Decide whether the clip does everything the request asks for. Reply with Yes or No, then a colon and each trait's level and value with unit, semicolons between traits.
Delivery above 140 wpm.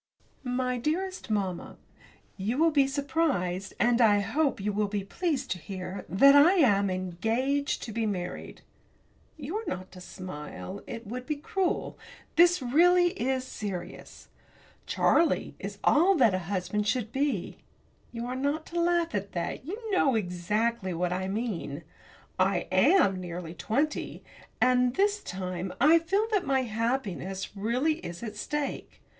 Yes: average, 150 wpm